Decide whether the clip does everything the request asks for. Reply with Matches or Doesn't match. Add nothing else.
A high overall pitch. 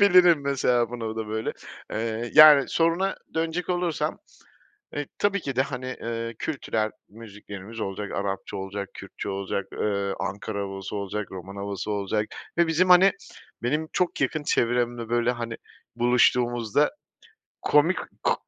Doesn't match